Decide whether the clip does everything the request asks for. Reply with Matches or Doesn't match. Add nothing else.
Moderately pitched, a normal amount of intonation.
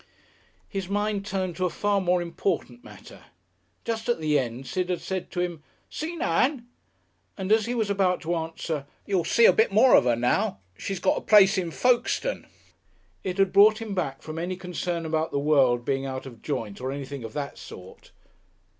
Doesn't match